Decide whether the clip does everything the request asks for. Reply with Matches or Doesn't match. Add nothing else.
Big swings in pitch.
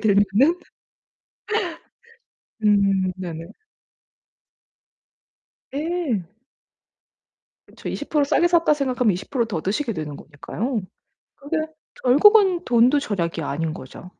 Matches